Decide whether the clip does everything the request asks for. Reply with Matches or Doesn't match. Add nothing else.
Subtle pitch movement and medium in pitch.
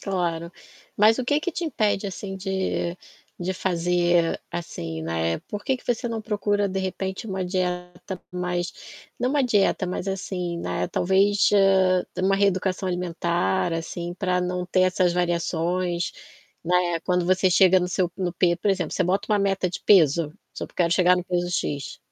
Matches